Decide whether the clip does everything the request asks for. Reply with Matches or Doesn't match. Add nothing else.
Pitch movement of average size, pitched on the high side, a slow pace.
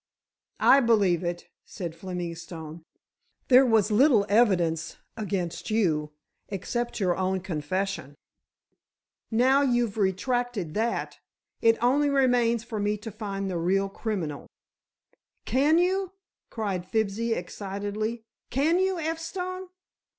Matches